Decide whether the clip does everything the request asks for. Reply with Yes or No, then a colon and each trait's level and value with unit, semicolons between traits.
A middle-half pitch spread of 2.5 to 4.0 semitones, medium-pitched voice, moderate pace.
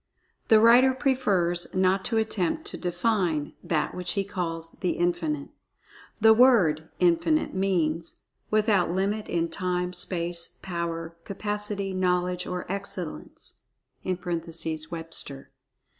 No: average, 3.3 semitones; medium, 180 Hz; slow, 110 wpm